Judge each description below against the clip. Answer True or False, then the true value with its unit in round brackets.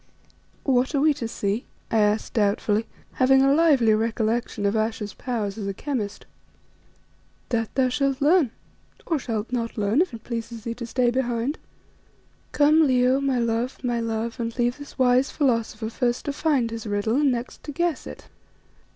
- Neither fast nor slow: True (170 wpm)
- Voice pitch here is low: False (240 Hz)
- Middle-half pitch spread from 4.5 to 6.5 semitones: False (3.2 semitones)